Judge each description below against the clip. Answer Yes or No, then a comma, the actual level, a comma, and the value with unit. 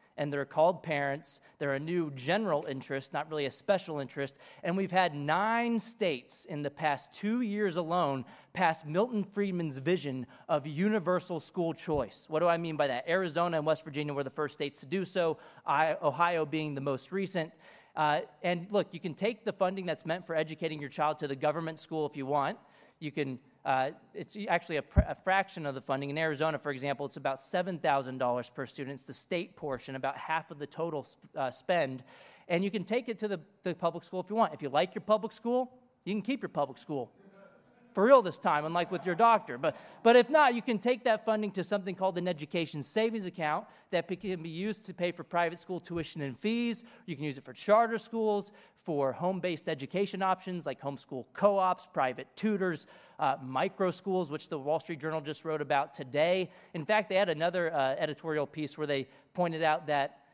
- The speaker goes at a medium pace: No, fast, 210 wpm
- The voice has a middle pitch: Yes, medium, 165 Hz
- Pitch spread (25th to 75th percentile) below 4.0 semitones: No, average, 4.7 semitones